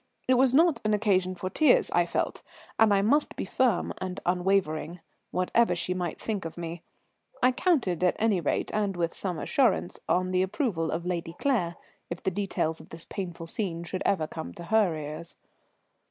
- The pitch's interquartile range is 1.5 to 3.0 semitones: No, average, 4.0 semitones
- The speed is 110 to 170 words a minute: No, average, 185 wpm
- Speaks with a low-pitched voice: No, medium, 185 Hz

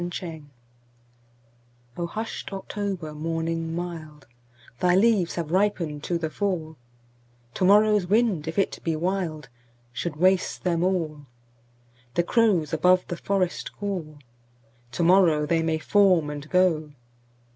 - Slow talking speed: Yes, slow, 115 wpm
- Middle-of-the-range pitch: Yes, medium, 165 Hz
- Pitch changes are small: No, wide, 5.4 semitones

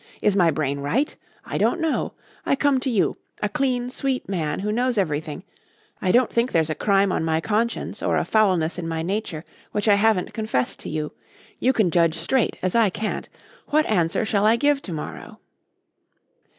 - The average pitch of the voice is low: No, high, 200 Hz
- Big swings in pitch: Yes, wide, 6.2 semitones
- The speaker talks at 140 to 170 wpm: No, average, 190 wpm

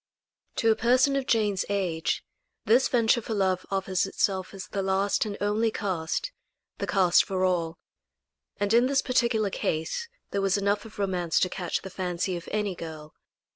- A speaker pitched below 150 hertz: No, high, 195 Hz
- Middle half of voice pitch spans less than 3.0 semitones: No, average, 3.3 semitones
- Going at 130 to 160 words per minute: No, average, 175 wpm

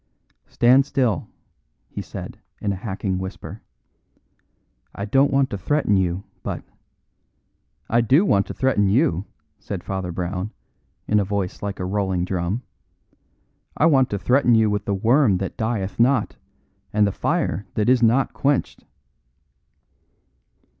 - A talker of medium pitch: No, low, 105 Hz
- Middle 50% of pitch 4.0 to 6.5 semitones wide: Yes, average, 4.7 semitones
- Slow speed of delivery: No, average, 145 wpm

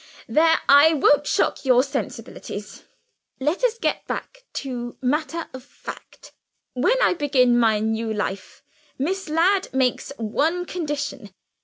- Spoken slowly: Yes, slow, 130 wpm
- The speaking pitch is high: Yes, very high, 285 Hz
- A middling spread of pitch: Yes, average, 5.0 semitones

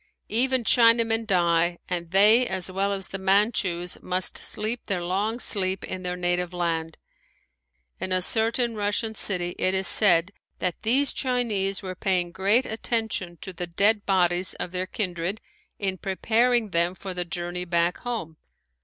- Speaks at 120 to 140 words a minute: No, average, 155 wpm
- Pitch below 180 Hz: No, high, 190 Hz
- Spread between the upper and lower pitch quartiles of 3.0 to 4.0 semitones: Yes, average, 3.6 semitones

